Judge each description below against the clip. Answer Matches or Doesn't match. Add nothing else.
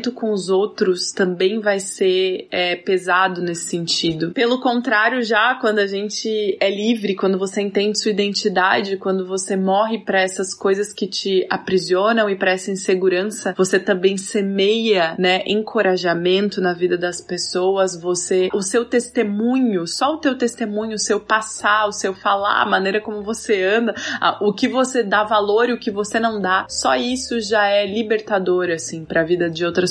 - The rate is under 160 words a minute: Doesn't match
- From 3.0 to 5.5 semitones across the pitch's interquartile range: Doesn't match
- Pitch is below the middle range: Doesn't match